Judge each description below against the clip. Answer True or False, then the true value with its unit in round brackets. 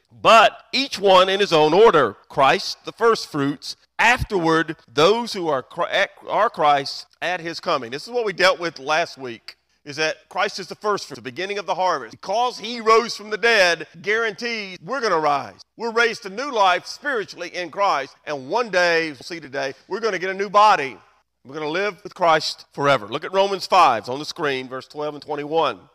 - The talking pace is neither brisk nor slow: False (210 wpm)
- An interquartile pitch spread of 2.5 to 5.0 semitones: False (5.6 semitones)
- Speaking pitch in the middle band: True (180 Hz)